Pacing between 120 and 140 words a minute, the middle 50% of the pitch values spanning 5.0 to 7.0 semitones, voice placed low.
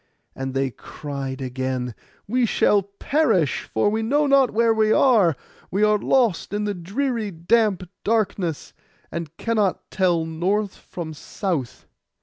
No: slow, 135 wpm; wide, 5.6 semitones; high, 195 Hz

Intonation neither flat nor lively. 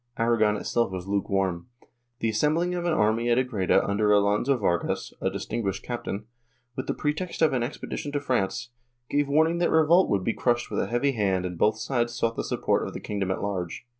No: wide, 5.7 semitones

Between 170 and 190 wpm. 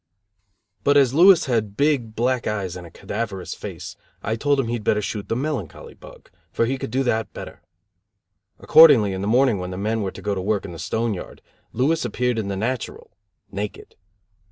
No: average, 200 wpm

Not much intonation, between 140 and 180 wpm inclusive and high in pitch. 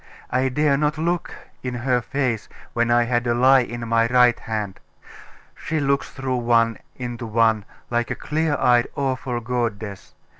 No: narrow, 2.3 semitones; average, 160 wpm; low, 120 Hz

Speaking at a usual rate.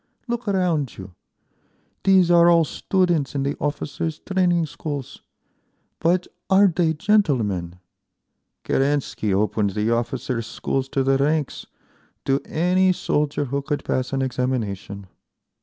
No: slow, 125 wpm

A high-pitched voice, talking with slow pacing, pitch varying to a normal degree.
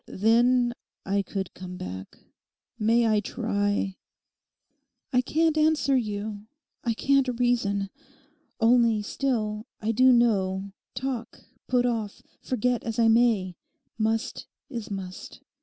Yes: high, 225 Hz; slow, 115 wpm; average, 3.3 semitones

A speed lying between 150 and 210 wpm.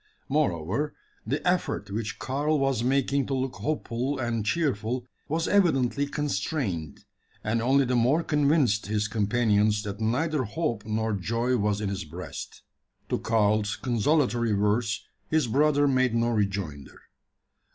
No: slow, 135 wpm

